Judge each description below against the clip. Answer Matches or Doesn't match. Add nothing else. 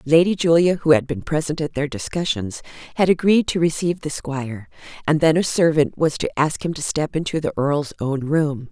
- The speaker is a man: Doesn't match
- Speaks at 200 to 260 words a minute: Matches